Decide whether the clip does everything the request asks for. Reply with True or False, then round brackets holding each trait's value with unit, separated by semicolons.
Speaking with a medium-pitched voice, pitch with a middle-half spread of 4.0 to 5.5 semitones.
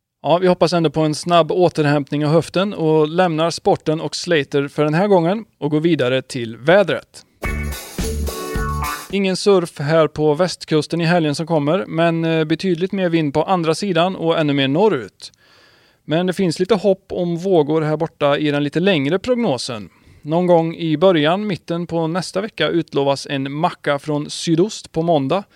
False (160 Hz; 3.3 semitones)